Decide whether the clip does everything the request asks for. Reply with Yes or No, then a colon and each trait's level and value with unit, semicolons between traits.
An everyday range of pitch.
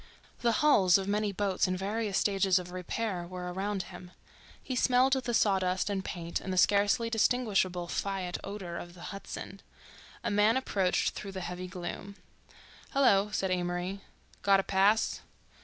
No: narrow, 2.3 semitones